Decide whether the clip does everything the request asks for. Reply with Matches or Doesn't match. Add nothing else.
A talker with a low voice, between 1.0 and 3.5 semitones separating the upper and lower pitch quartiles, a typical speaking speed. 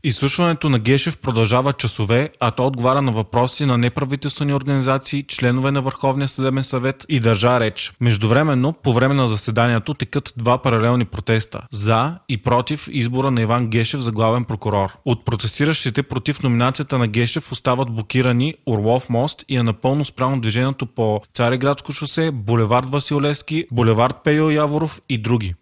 Matches